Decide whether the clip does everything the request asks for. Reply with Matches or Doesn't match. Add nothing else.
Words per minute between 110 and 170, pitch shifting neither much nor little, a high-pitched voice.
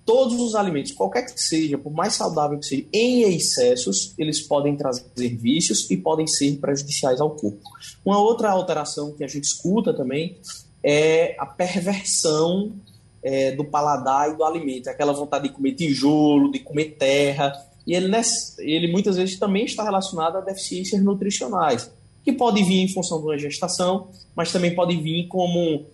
Doesn't match